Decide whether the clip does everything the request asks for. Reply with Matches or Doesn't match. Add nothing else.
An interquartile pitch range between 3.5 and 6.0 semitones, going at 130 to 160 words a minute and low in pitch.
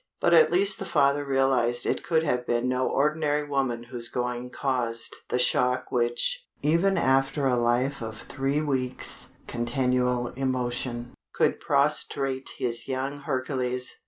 Doesn't match